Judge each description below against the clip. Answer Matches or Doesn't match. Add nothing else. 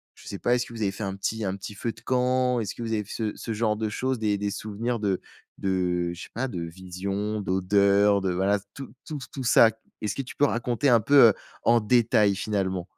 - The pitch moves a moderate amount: Matches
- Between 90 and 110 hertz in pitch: Matches